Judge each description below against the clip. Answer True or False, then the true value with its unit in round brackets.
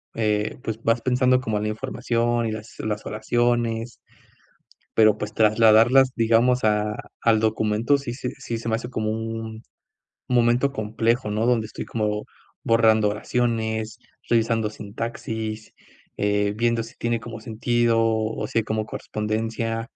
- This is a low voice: True (115 Hz)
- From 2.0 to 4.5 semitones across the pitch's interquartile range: False (1.5 semitones)